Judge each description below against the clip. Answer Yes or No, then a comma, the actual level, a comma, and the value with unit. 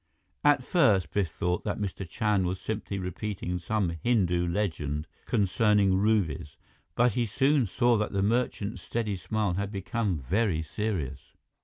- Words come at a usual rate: Yes, average, 145 wpm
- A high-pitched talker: No, low, 100 Hz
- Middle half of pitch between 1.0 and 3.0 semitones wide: No, average, 3.7 semitones